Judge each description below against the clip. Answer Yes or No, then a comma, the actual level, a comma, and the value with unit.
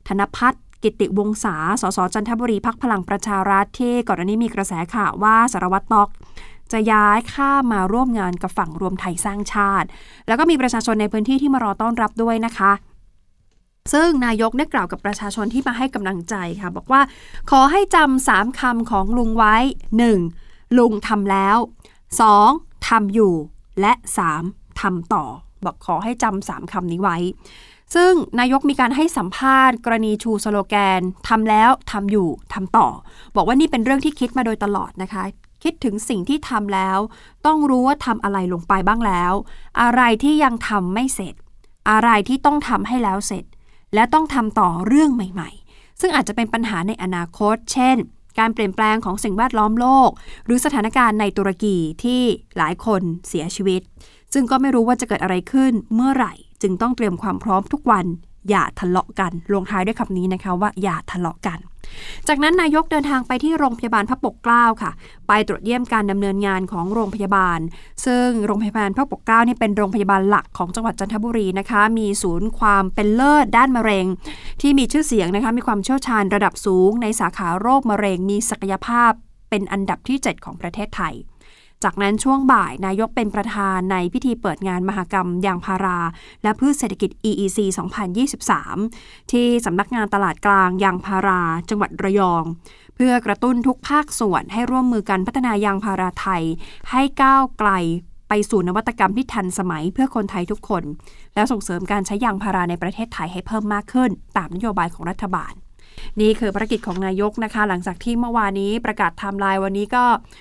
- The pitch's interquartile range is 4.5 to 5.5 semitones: No, average, 3.7 semitones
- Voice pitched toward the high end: Yes, high, 210 Hz